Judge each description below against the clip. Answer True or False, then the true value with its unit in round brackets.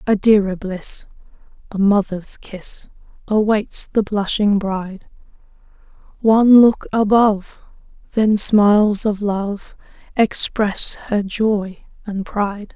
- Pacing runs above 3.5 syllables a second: False (3.4 syllables/s)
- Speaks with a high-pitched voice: True (205 Hz)